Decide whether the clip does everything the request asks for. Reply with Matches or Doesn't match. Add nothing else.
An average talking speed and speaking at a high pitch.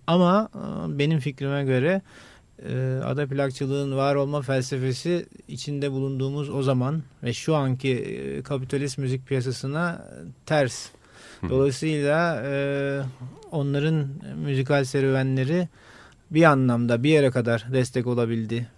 Doesn't match